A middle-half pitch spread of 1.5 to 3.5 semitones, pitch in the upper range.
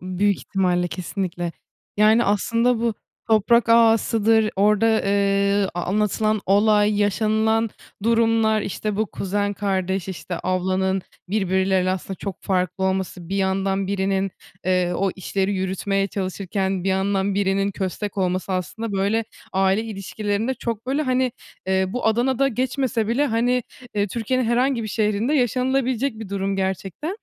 Yes: average, 2.9 semitones; high, 200 Hz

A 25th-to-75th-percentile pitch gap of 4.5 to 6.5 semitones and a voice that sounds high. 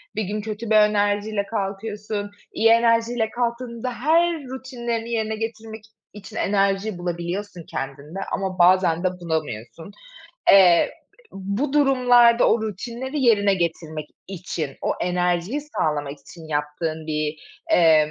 Yes: average, 5.1 semitones; high, 205 Hz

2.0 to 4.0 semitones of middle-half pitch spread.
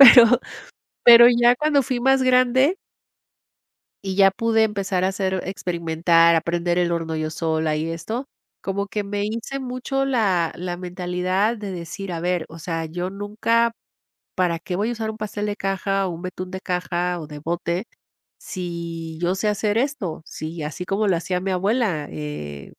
No: average, 4.4 semitones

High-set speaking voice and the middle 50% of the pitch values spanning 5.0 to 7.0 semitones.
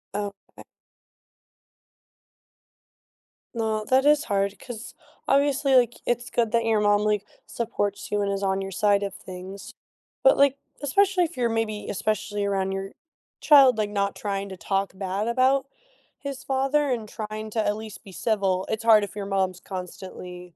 No: high, 210 Hz; average, 3.6 semitones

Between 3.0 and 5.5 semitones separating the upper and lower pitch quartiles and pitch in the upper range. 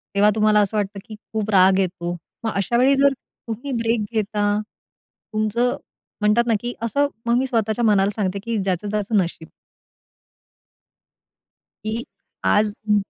No: narrow, 2.5 semitones; high, 215 Hz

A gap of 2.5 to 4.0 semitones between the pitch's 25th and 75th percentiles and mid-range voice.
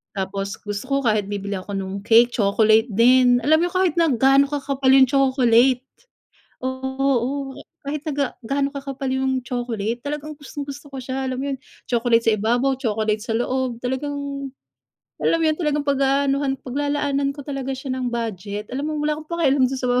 No: average, 3.3 semitones; very high, 265 Hz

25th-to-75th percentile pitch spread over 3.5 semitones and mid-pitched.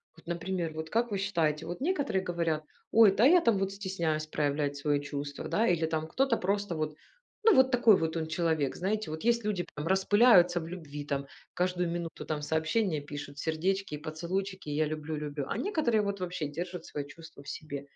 Yes: average, 4.4 semitones; medium, 170 Hz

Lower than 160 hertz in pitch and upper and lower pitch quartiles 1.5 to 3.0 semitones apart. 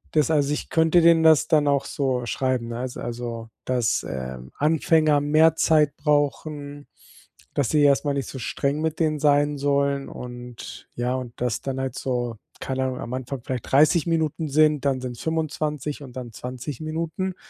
No: medium, 140 Hz; average, 3.4 semitones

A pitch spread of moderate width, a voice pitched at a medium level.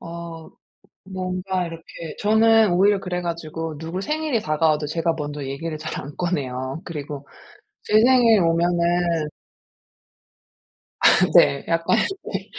Yes: average, 3.2 semitones; medium, 170 Hz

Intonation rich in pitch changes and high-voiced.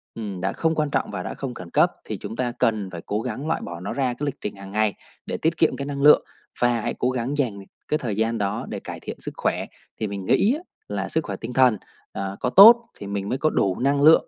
No: wide, 5.9 semitones; low, 115 Hz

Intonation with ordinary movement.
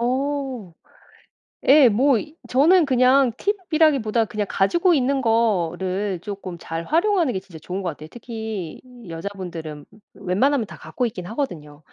No: wide, 6.9 semitones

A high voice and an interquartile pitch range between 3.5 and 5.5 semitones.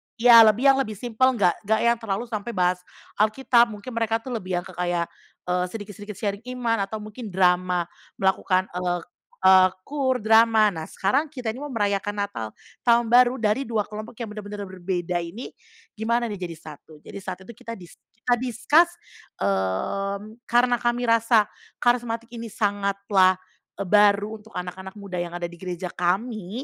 Yes: high, 210 Hz; average, 3.9 semitones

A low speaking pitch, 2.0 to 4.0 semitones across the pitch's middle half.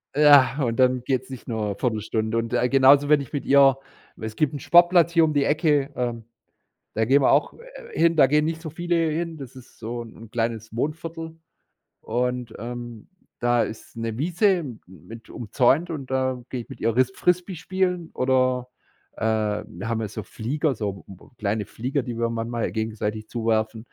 No: low, 125 Hz; average, 5.0 semitones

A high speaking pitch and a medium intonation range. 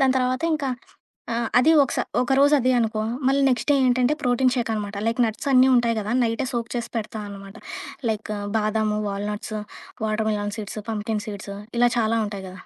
Yes: high, 225 Hz; average, 3.0 semitones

